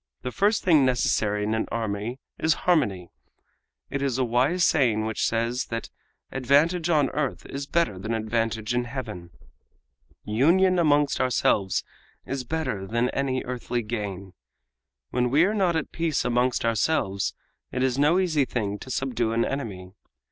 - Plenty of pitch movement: No, average, 4.9 semitones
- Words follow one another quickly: No, average, 155 wpm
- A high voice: No, low, 125 Hz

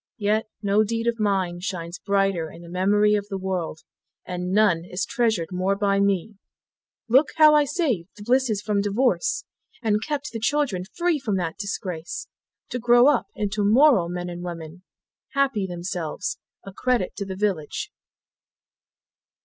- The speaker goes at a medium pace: Yes, average, 155 wpm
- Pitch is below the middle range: No, high, 200 Hz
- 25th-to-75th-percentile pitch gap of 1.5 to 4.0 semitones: No, average, 4.5 semitones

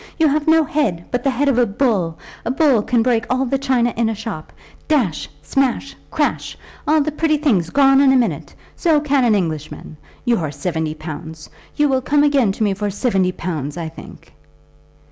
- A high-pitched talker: Yes, high, 240 Hz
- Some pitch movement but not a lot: No, wide, 7.5 semitones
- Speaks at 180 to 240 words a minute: Yes, average, 195 wpm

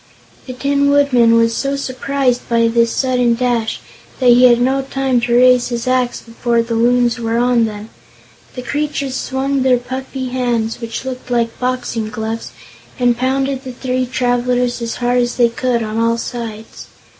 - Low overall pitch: No, high, 245 Hz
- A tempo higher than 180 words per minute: No, average, 170 wpm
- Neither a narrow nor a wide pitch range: No, narrow, 1.7 semitones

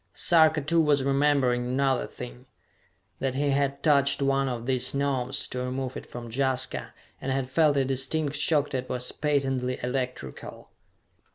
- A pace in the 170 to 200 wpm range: No, average, 155 wpm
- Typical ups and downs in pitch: No, narrow, 1.9 semitones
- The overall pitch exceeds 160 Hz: No, low, 135 Hz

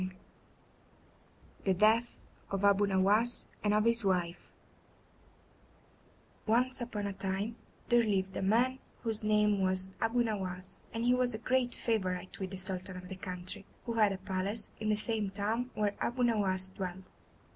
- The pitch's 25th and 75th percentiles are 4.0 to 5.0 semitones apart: No, average, 3.3 semitones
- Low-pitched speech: No, high, 205 Hz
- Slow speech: No, average, 160 wpm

